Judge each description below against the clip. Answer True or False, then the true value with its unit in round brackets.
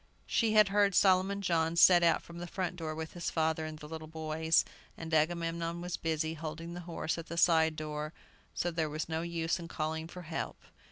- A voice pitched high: False (165 Hz)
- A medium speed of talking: False (210 wpm)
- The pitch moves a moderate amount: False (1.6 semitones)